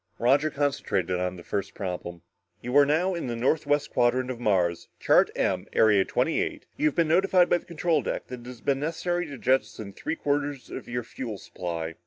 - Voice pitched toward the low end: Yes, low, 125 Hz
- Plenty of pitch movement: Yes, wide, 7.1 semitones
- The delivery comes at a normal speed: No, fast, 210 wpm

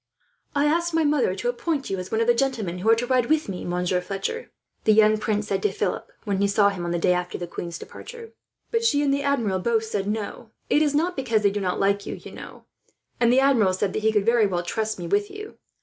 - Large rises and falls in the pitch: Yes, wide, 5.9 semitones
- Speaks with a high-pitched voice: Yes, high, 215 Hz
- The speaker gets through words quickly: Yes, fast, 260 wpm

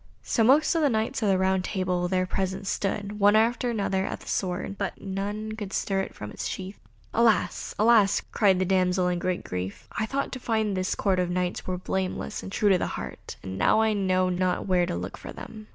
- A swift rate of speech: Yes, fast, 225 wpm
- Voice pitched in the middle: No, high, 195 Hz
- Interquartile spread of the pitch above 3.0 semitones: No, average, 2.7 semitones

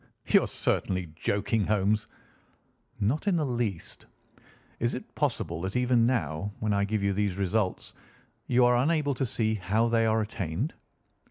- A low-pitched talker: Yes, low, 110 Hz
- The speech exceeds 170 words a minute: No, average, 160 wpm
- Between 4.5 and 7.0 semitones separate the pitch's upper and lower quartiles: No, average, 3.6 semitones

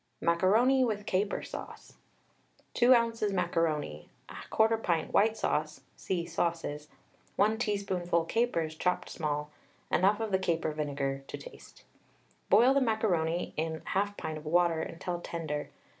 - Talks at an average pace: No, slow, 130 wpm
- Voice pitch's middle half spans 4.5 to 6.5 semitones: Yes, average, 5.3 semitones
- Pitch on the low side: No, medium, 175 Hz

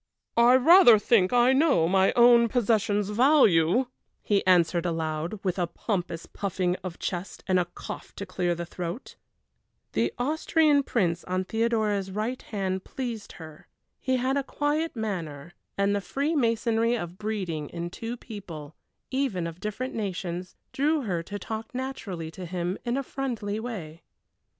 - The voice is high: Yes, high, 205 Hz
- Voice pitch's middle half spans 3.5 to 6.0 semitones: Yes, wide, 5.5 semitones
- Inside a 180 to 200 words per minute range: No, average, 155 wpm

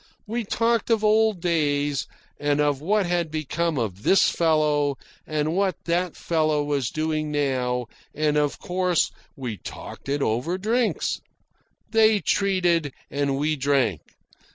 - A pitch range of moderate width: Yes, average, 4.3 semitones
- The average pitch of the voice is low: No, medium, 155 Hz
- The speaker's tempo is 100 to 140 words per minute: Yes, slow, 135 wpm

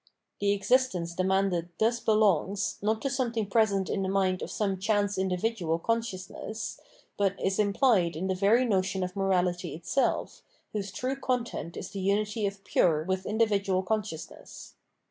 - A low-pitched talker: No, high, 195 Hz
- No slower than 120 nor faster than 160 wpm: Yes, average, 155 wpm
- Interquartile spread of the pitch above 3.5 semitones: No, average, 2.7 semitones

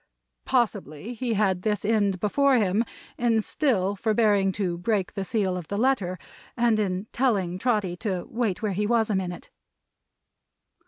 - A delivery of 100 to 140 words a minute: No, average, 155 wpm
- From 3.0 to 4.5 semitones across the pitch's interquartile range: Yes, average, 3.4 semitones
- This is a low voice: No, high, 210 Hz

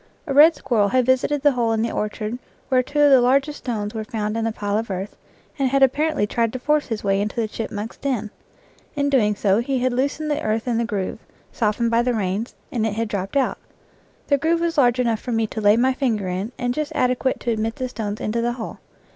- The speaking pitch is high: Yes, high, 235 Hz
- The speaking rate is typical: No, fast, 245 wpm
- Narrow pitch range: No, average, 3.6 semitones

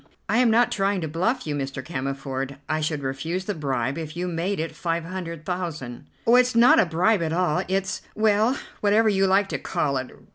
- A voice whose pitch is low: No, medium, 170 Hz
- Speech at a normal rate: No, fast, 210 wpm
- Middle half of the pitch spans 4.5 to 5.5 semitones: Yes, average, 5.2 semitones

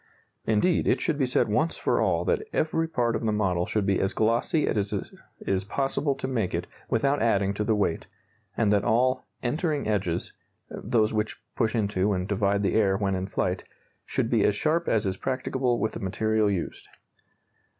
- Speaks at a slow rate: No, average, 190 wpm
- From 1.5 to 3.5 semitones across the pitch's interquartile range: No, average, 4.5 semitones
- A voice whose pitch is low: Yes, low, 110 Hz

